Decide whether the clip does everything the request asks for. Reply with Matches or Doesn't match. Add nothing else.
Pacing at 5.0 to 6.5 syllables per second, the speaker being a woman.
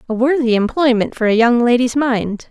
Matches